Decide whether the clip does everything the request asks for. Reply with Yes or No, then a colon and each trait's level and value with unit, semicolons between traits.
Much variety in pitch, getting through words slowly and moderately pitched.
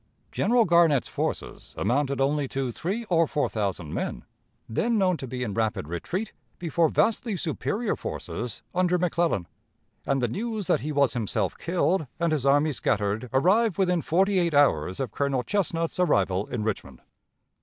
No: wide, 6.7 semitones; average, 160 wpm; medium, 150 Hz